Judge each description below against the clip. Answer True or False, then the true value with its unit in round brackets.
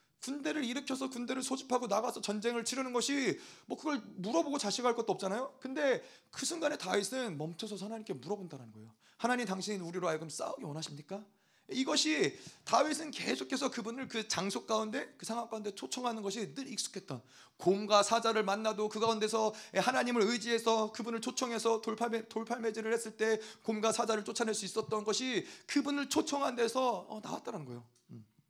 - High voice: True (225 Hz)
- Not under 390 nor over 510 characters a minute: True (395 characters per minute)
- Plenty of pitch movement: False (3.7 semitones)